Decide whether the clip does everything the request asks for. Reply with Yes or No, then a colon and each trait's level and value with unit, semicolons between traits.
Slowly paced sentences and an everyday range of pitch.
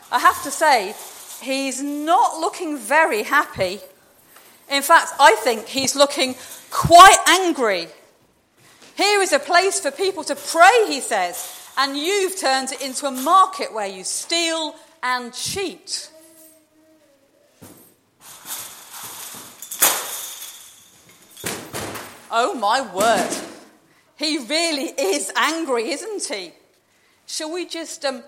Yes: slow, 110 wpm; average, 3.9 semitones